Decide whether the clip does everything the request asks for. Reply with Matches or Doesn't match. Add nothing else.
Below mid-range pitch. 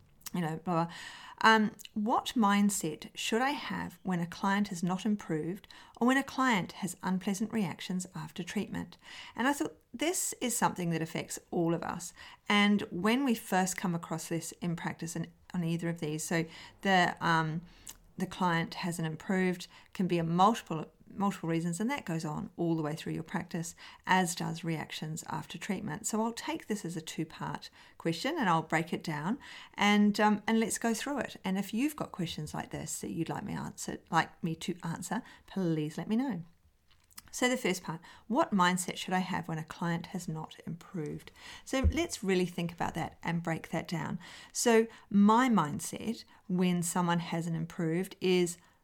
Doesn't match